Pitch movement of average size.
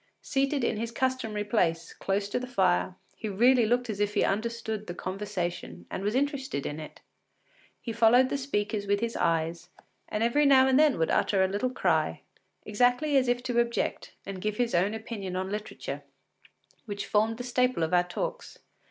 Yes: average, 4.2 semitones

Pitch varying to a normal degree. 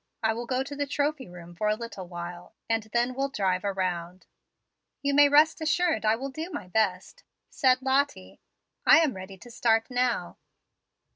No: wide, 6.8 semitones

